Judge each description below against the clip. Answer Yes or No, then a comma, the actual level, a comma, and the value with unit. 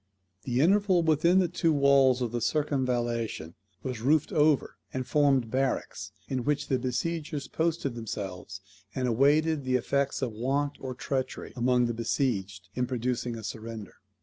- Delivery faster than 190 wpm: No, average, 150 wpm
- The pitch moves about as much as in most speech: Yes, average, 3.7 semitones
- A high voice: No, low, 130 Hz